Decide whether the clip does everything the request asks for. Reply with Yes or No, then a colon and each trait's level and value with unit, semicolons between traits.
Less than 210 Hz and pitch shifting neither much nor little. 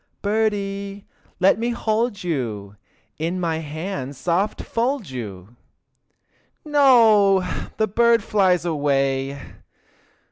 No: high, 190 Hz; wide, 7.2 semitones